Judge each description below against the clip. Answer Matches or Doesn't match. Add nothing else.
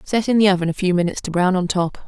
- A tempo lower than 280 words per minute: Doesn't match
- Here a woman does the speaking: Matches